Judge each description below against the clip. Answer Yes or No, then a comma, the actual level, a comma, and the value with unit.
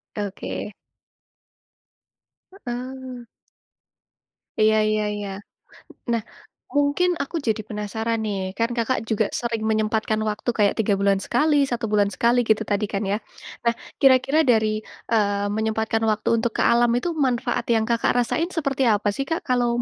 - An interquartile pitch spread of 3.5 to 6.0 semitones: No, average, 2.7 semitones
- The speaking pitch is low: No, high, 225 Hz